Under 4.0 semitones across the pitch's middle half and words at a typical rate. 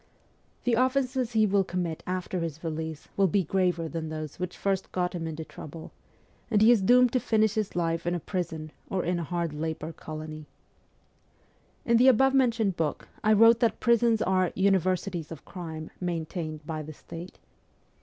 No: average, 5.1 semitones; average, 180 wpm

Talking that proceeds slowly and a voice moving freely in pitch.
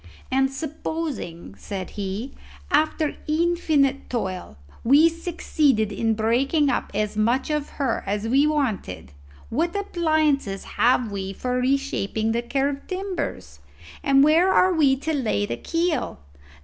Yes: slow, 130 wpm; wide, 6.1 semitones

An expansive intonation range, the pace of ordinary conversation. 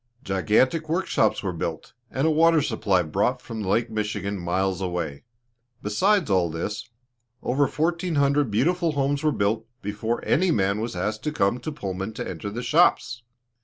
Yes: wide, 7.1 semitones; average, 165 wpm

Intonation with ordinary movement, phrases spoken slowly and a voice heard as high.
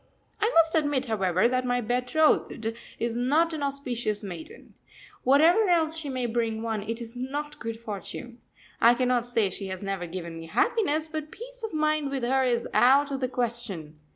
No: average, 4.9 semitones; average, 185 wpm; very high, 250 Hz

